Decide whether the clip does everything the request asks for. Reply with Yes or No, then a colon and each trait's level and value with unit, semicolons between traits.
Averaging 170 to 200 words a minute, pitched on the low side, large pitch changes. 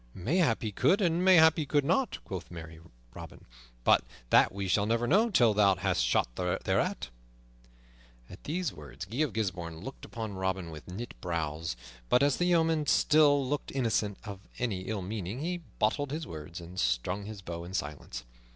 Yes: average, 180 wpm; low, 105 Hz; wide, 8.5 semitones